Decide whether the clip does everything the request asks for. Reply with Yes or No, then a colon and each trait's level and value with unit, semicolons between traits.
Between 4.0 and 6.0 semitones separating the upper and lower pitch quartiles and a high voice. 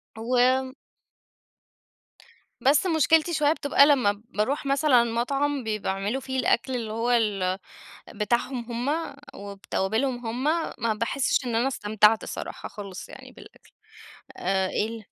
Yes: average, 4.3 semitones; high, 240 Hz